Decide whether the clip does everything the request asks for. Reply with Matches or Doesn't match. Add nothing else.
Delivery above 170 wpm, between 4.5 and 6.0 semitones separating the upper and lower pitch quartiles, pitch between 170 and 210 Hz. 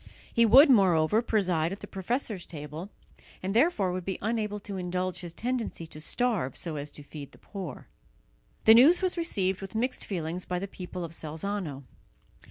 Matches